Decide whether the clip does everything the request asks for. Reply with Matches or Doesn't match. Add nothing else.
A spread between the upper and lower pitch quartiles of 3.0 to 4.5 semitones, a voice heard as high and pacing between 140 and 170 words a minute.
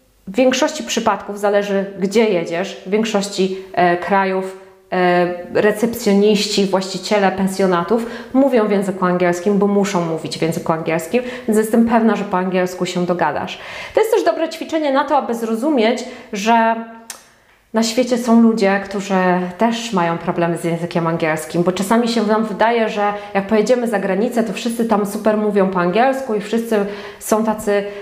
Matches